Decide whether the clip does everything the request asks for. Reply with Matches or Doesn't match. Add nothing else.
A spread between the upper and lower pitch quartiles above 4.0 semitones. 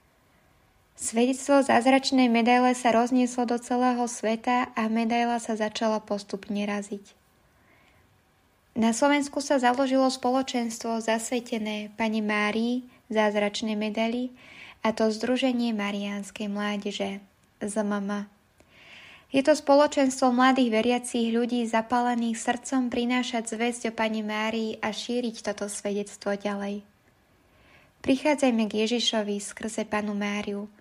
Doesn't match